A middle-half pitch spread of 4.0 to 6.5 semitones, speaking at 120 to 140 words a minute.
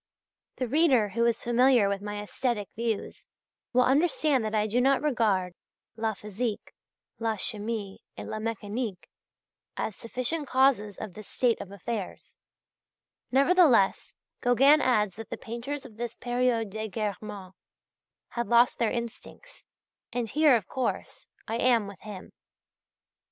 No: average, 3.3 semitones; slow, 135 wpm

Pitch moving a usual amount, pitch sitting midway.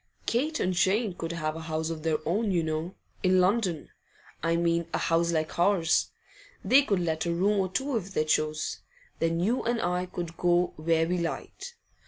Yes: average, 3.0 semitones; medium, 175 Hz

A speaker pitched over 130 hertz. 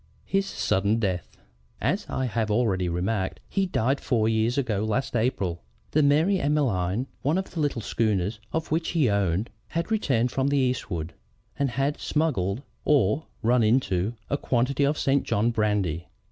No: low, 120 Hz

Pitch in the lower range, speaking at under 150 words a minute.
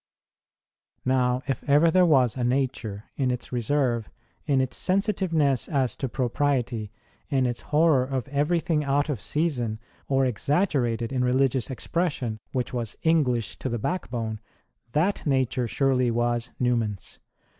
Yes: low, 130 Hz; average, 140 wpm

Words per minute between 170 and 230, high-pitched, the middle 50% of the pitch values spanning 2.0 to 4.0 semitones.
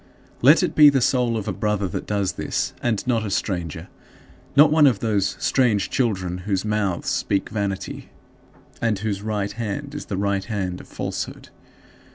No: average, 175 wpm; low, 105 Hz; average, 3.6 semitones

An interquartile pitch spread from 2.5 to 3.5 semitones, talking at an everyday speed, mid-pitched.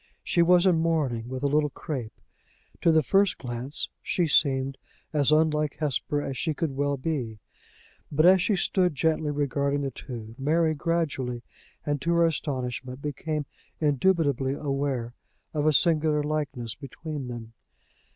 Yes: average, 3.2 semitones; average, 150 wpm; medium, 145 Hz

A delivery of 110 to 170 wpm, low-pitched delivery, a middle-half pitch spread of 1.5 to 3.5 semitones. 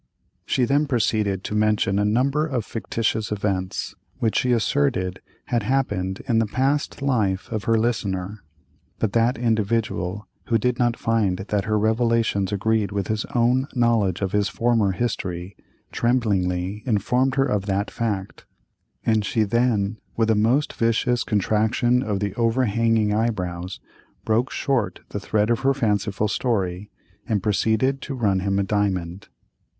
Yes: average, 150 wpm; low, 110 Hz; average, 3.1 semitones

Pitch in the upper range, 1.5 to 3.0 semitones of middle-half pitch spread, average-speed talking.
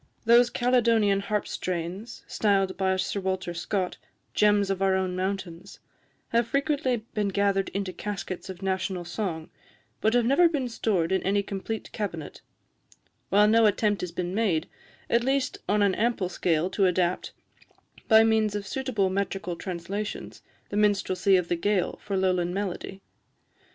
Yes: high, 195 Hz; average, 2.7 semitones; average, 150 wpm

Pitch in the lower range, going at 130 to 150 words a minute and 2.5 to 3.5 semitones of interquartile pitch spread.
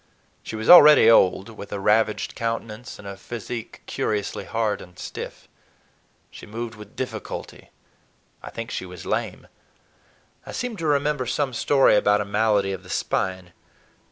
Yes: low, 110 Hz; average, 145 wpm; average, 3.1 semitones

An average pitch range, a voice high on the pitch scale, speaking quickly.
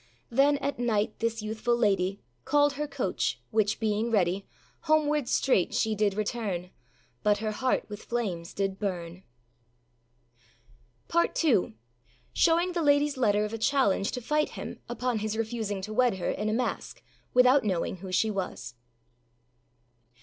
No: average, 4.5 semitones; high, 220 Hz; average, 150 wpm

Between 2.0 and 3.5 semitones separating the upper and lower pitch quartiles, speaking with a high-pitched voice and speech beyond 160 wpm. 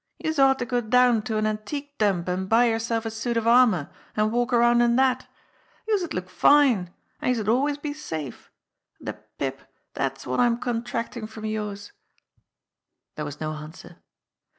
Yes: average, 3.0 semitones; high, 230 Hz; average, 170 wpm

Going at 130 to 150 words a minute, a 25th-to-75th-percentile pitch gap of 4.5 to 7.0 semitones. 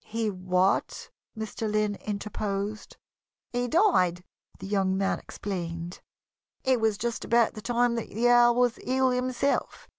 No: average, 140 wpm; average, 3.7 semitones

